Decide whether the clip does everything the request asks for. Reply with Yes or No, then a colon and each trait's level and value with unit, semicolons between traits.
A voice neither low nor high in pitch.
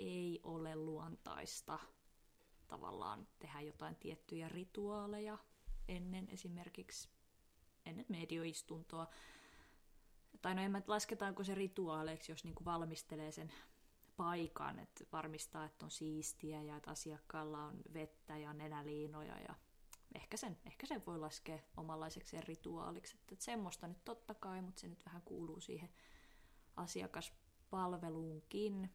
Yes: medium, 165 Hz